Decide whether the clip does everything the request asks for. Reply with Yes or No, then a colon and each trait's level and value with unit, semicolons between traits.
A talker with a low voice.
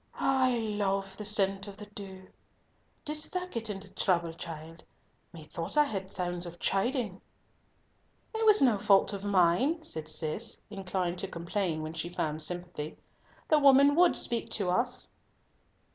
No: high, 195 Hz